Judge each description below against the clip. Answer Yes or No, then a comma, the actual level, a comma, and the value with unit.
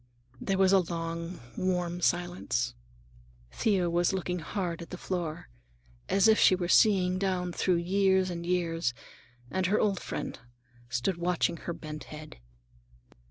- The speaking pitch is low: No, medium, 180 Hz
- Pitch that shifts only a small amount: Yes, narrow, 1.9 semitones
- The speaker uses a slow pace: No, average, 145 wpm